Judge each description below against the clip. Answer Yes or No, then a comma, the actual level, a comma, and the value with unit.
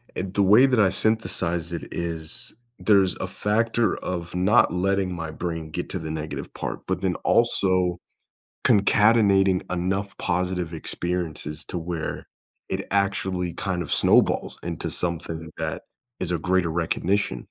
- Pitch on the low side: Yes, very low, 90 Hz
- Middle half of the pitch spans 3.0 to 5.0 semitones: No, narrow, 2.5 semitones